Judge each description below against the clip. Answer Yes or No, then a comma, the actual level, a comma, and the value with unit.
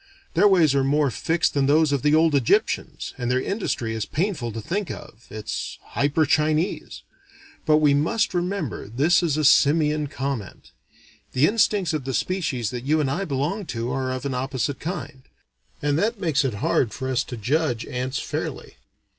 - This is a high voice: No, medium, 145 Hz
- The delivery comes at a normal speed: Yes, average, 180 wpm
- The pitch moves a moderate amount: Yes, average, 3.9 semitones